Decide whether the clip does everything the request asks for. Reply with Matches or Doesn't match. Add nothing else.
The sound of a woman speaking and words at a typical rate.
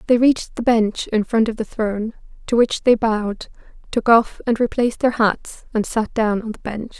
Doesn't match